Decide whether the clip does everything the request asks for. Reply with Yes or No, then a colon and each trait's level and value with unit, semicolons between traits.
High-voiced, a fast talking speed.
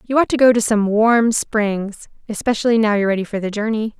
Yes: high, 220 Hz; fast, 225 wpm